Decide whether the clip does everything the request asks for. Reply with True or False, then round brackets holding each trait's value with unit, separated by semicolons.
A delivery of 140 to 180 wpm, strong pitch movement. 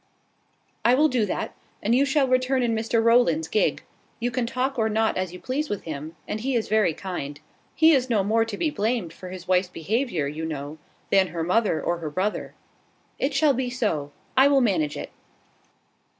False (200 wpm; 6.6 semitones)